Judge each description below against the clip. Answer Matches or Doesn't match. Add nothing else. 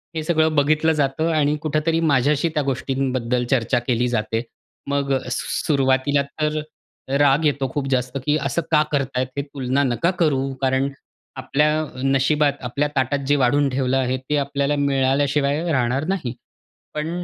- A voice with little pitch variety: Matches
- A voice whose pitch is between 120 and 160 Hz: Matches